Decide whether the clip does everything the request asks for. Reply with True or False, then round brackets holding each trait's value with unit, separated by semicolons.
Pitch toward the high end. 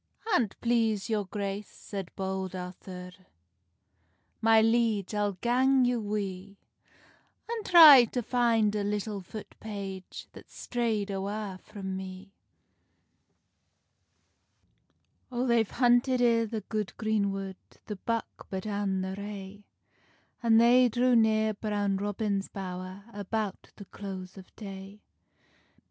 True (205 Hz)